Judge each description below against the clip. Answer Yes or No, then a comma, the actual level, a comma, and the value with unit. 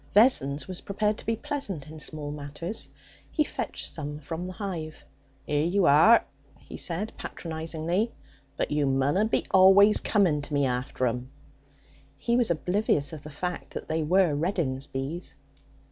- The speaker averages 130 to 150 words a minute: No, average, 160 wpm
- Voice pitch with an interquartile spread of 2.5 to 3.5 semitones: No, average, 5.2 semitones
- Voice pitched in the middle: Yes, medium, 165 Hz